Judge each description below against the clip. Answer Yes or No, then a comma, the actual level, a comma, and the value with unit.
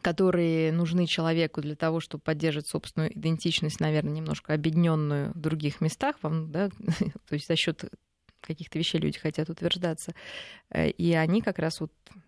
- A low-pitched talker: No, medium, 165 Hz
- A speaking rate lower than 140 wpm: No, average, 150 wpm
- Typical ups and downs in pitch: No, narrow, 1.6 semitones